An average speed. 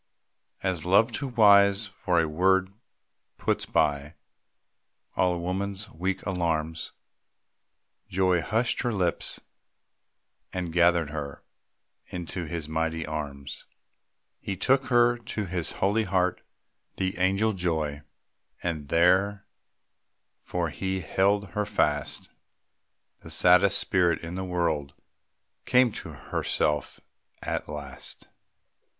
No: slow, 105 wpm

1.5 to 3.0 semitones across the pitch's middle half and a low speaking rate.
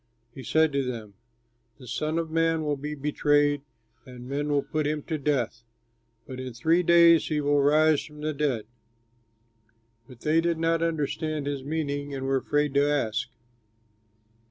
No: narrow, 2.5 semitones; average, 165 wpm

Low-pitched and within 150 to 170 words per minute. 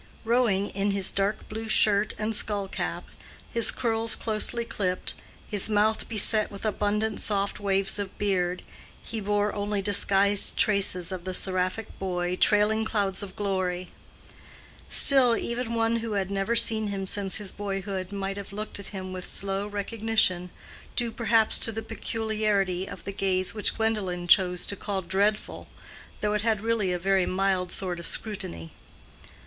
No: high, 200 Hz; average, 160 wpm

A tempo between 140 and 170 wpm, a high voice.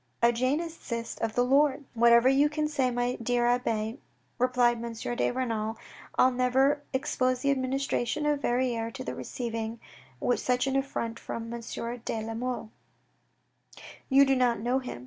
Yes: average, 155 wpm; very high, 250 Hz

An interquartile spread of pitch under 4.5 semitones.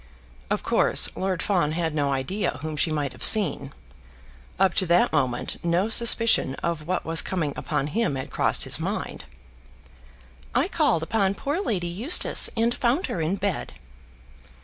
No: average, 5.2 semitones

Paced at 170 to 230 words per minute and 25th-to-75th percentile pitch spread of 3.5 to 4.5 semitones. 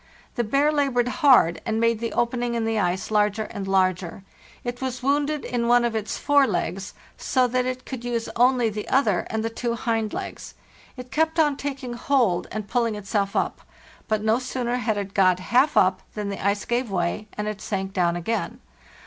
Yes: average, 200 wpm; average, 3.8 semitones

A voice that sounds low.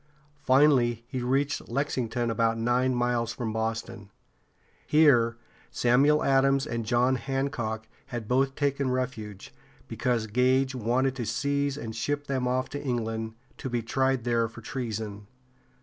Yes: low, 125 Hz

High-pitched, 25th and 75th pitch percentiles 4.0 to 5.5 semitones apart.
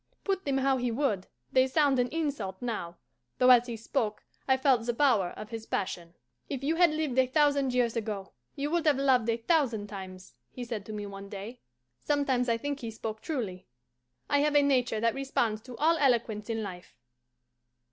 Yes: high, 245 Hz; average, 4.5 semitones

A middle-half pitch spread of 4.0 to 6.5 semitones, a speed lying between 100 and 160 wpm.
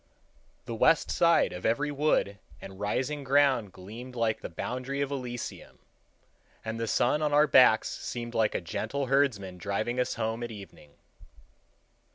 Yes: average, 4.3 semitones; average, 155 wpm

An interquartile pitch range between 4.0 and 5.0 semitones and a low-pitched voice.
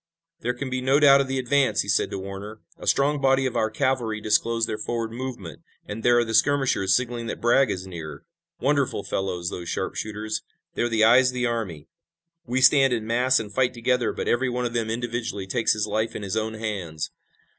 No: average, 3.2 semitones; low, 115 Hz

